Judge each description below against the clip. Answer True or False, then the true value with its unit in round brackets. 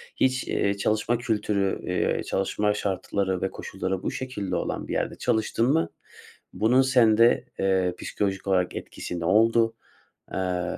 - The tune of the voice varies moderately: True (3.3 semitones)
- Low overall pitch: True (100 Hz)